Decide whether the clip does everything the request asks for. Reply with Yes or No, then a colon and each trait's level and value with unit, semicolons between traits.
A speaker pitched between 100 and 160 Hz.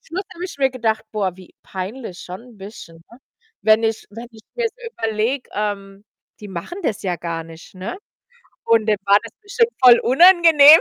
No: high, 220 Hz